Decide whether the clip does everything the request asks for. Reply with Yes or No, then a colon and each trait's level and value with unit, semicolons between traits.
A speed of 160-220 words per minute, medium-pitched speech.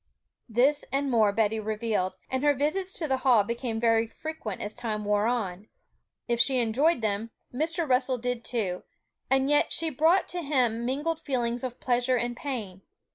No: average, 175 wpm; high, 245 Hz